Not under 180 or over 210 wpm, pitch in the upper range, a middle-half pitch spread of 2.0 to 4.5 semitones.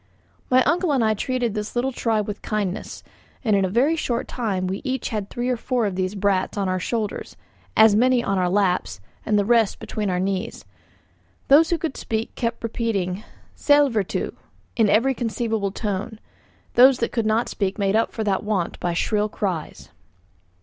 Yes: average, 185 wpm; high, 215 Hz; average, 3.6 semitones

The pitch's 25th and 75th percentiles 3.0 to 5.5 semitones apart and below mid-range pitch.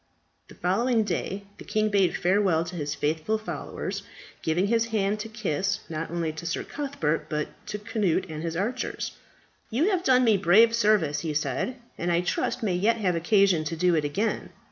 No: average, 4.9 semitones; high, 190 Hz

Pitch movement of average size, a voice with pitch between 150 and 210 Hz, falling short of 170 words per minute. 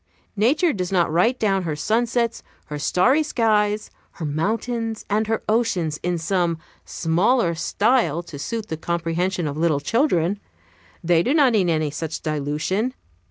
No: wide, 5.7 semitones; medium, 185 Hz; average, 150 wpm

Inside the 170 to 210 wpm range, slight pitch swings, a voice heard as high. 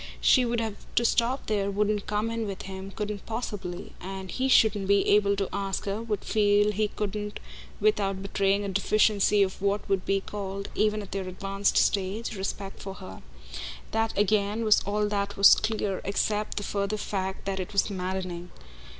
Yes: average, 180 wpm; narrow, 1.4 semitones; high, 200 Hz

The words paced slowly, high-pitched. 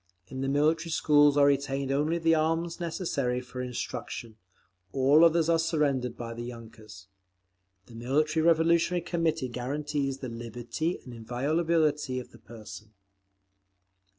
No: slow, 130 wpm; medium, 140 Hz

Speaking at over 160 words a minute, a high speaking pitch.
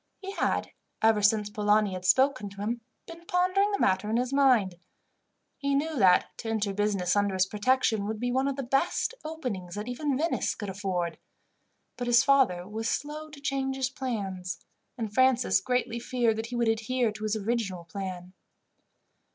Yes: average, 180 wpm; high, 225 Hz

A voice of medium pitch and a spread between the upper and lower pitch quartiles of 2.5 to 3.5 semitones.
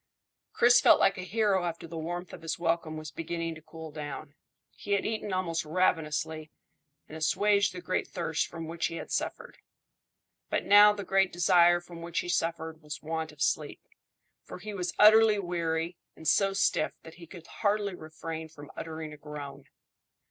Yes: medium, 170 Hz; average, 2.9 semitones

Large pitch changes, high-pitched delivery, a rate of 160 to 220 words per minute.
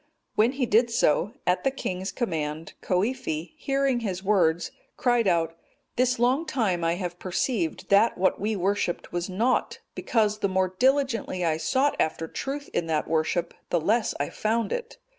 Yes: wide, 5.9 semitones; high, 200 Hz; average, 165 wpm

